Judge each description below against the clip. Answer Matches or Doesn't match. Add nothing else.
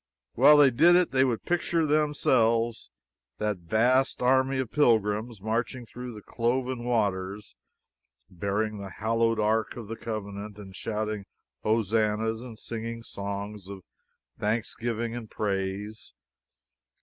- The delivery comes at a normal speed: Doesn't match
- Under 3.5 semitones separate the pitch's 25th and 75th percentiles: Matches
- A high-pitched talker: Doesn't match